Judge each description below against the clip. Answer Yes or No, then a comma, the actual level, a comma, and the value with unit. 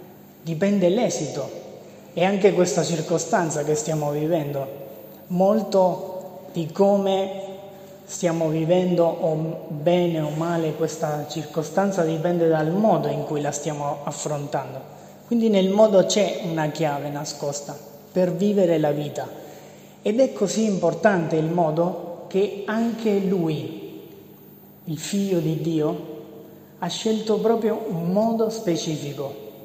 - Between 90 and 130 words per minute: Yes, slow, 115 wpm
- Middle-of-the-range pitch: Yes, medium, 170 Hz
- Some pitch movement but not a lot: Yes, average, 3.9 semitones